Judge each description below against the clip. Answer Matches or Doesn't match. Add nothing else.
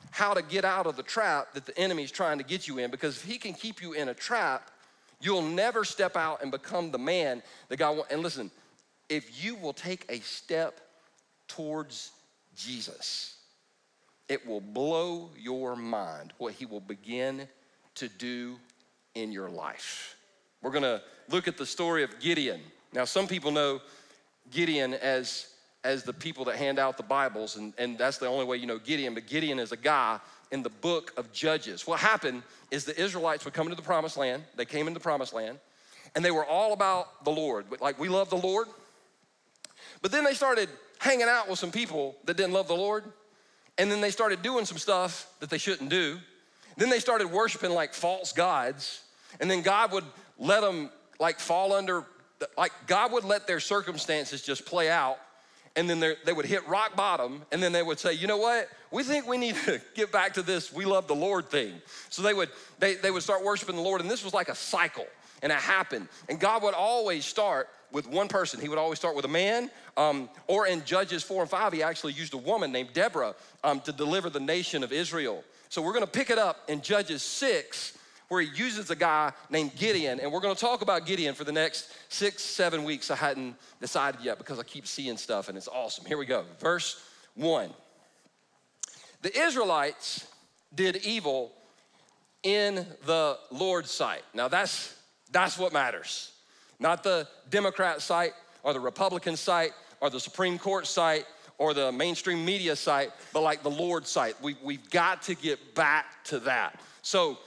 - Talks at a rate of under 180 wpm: Doesn't match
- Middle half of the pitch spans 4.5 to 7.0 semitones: Matches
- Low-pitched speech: Doesn't match